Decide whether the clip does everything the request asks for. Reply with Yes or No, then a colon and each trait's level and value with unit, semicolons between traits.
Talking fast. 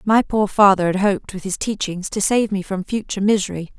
Yes: fast, 220 wpm